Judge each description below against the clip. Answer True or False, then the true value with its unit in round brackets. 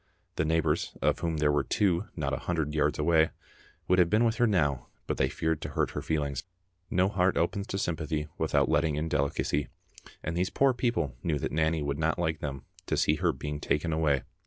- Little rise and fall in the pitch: False (3.0 semitones)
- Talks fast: True (210 wpm)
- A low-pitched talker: True (80 Hz)